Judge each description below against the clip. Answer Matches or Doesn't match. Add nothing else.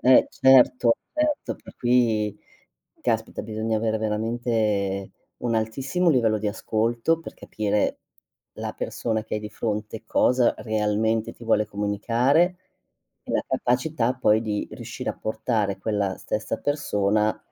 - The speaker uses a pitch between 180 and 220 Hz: Doesn't match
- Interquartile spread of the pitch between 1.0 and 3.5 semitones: Matches